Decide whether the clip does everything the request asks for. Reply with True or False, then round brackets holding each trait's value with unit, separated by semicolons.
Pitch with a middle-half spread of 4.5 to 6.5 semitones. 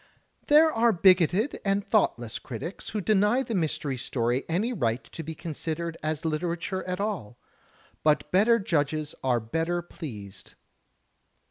True (5.5 semitones)